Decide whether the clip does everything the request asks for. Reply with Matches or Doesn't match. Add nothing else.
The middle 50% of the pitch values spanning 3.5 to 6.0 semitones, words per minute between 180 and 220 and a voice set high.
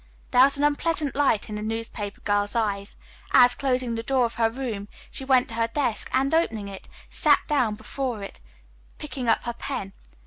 Matches